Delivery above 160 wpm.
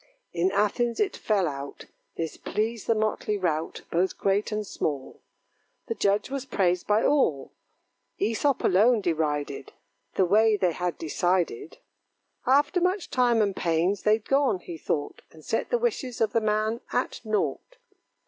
No: average, 150 wpm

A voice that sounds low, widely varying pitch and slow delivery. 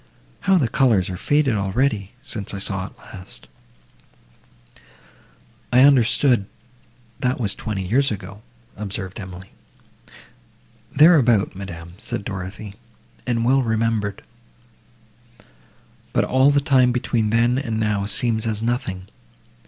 No: low, 110 Hz; average, 4.2 semitones; slow, 115 wpm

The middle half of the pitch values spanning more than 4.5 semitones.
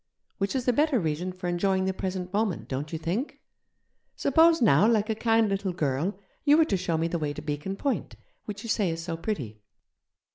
Yes: average, 5.2 semitones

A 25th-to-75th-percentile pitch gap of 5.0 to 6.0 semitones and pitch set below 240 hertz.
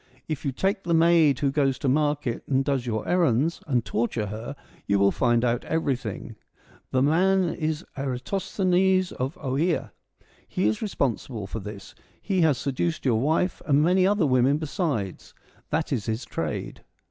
Yes: wide, 5.6 semitones; medium, 140 Hz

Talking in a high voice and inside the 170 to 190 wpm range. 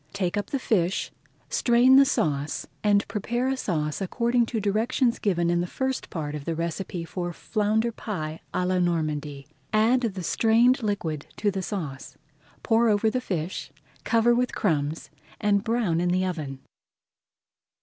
No: high, 200 Hz; average, 160 wpm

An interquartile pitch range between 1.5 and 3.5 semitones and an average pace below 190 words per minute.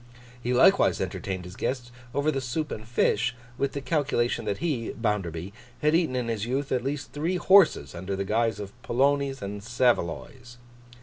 No: average, 5.0 semitones; average, 175 wpm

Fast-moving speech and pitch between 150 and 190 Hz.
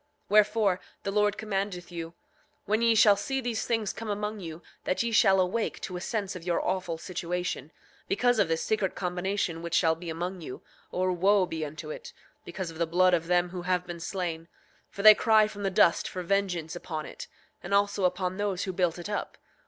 Yes: fast, 210 wpm; medium, 185 Hz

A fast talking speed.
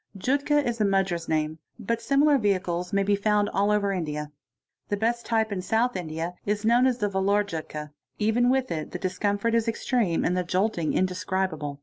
No: average, 190 wpm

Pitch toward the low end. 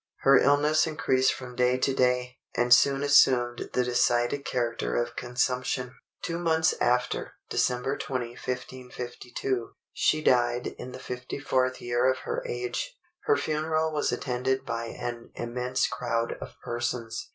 Yes: low, 125 Hz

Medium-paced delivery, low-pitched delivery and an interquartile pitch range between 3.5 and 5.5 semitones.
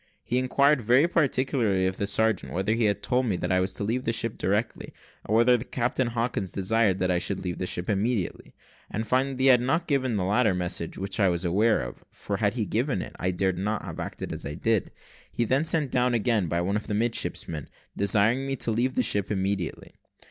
No: fast, 230 wpm; low, 110 Hz; average, 4.6 semitones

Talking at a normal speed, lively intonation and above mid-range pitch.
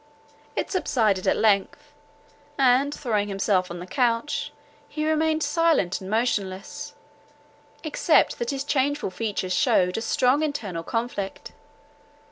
No: slow, 120 wpm; wide, 6.9 semitones; high, 240 Hz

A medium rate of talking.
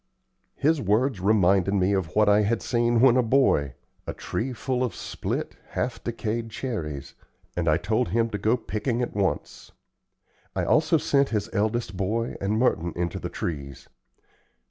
Yes: average, 165 wpm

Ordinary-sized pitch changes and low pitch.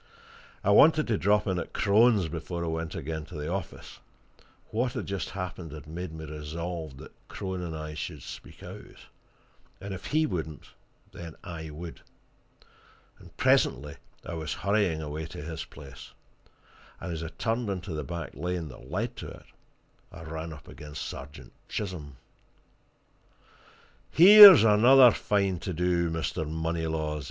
Yes: average, 4.0 semitones; very low, 85 Hz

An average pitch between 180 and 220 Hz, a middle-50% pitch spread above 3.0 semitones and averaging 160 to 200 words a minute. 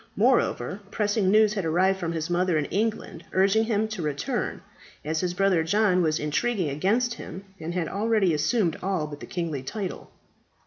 Yes: medium, 185 Hz; average, 4.5 semitones; average, 175 wpm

